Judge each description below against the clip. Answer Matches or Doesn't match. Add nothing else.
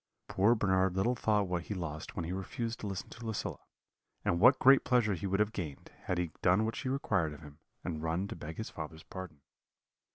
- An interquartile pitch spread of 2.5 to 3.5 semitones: Doesn't match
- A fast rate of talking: Matches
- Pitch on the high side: Doesn't match